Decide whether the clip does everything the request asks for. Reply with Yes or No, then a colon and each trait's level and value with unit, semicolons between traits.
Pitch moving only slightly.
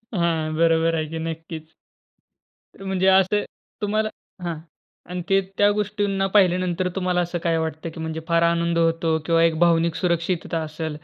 Yes: narrow, 2.2 semitones